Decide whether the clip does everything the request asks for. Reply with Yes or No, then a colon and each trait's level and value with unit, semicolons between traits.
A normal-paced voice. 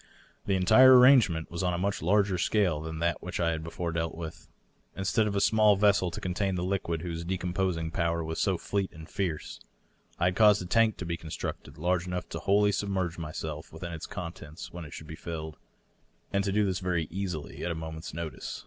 No: fast, 215 wpm